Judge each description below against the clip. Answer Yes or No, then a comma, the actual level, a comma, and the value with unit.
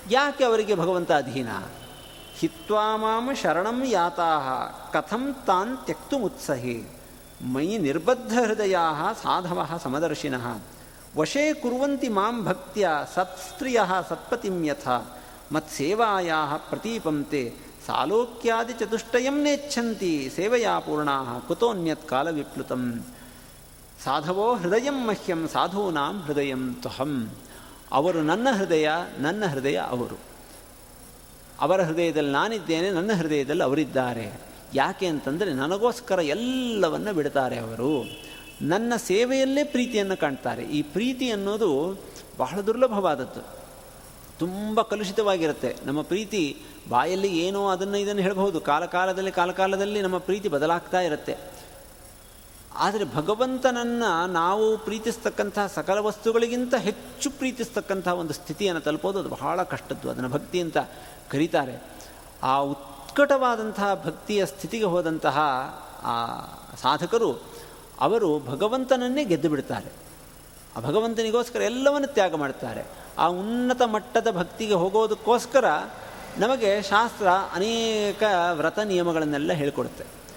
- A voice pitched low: No, high, 190 Hz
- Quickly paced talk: No, average, 90 wpm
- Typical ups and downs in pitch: No, wide, 6.6 semitones